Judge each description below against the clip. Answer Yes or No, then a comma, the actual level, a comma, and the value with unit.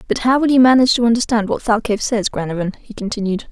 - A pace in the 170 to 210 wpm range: No, fast, 220 wpm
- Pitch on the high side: Yes, high, 225 Hz